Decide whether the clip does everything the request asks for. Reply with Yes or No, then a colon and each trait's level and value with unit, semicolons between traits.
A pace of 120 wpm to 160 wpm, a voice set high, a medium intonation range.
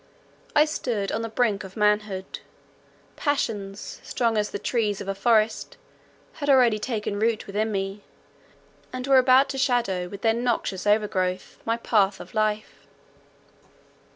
Yes: average, 145 wpm; high, 215 Hz; average, 3.3 semitones